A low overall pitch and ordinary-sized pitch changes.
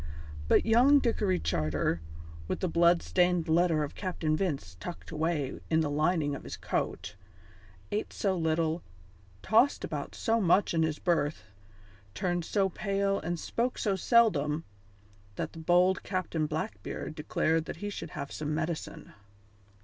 No: medium, 170 Hz; average, 3.7 semitones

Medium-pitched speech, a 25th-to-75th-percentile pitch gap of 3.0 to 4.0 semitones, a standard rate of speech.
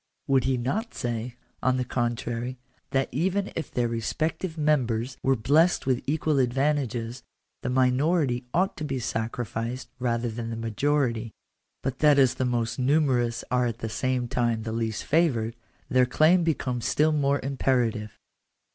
No: low, 125 Hz; average, 3.4 semitones; average, 160 wpm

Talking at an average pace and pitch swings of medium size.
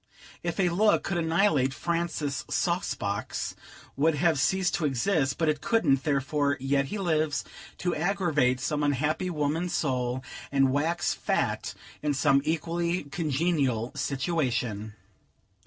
No: slow, 125 wpm; average, 4.1 semitones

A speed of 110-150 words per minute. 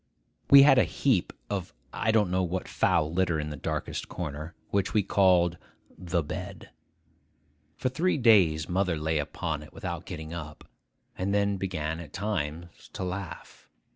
No: average, 160 wpm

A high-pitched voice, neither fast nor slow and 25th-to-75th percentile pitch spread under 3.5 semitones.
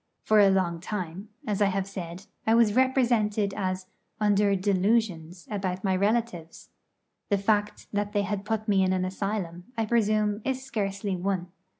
Yes: high, 200 Hz; average, 160 wpm; narrow, 2.4 semitones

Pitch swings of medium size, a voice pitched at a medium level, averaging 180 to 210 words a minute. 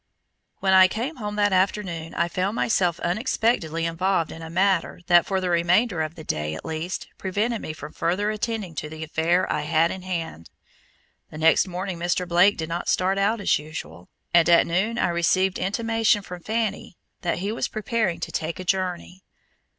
Yes: average, 3.4 semitones; medium, 180 Hz; average, 190 wpm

